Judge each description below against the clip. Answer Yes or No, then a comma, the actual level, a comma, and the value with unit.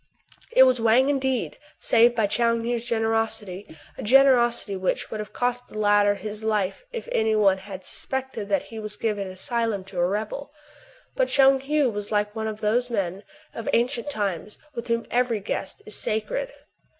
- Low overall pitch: No, high, 220 Hz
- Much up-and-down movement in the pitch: No, average, 3.0 semitones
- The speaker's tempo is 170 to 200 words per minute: Yes, average, 185 wpm